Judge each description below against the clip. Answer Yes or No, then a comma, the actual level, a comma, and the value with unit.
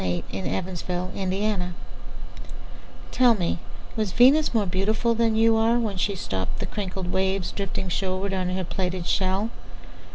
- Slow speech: Yes, slow, 120 wpm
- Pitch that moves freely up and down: No, average, 3.3 semitones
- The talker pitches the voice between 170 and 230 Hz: Yes, high, 190 Hz